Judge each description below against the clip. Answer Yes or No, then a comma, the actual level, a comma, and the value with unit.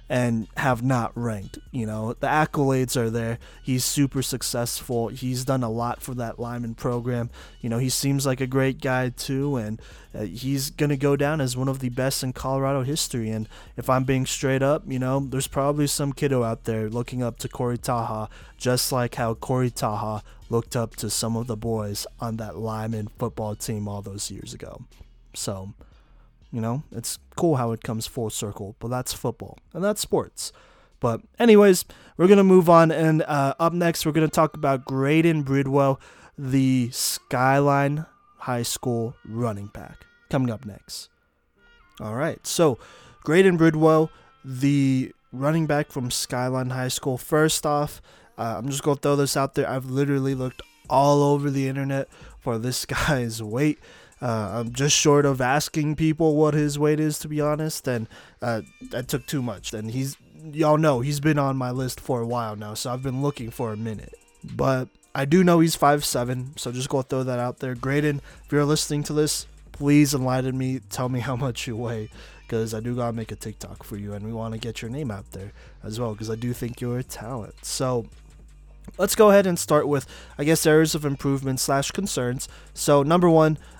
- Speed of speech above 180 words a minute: Yes, average, 195 wpm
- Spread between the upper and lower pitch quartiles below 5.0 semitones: Yes, average, 3.7 semitones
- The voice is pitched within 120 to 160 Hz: Yes, low, 130 Hz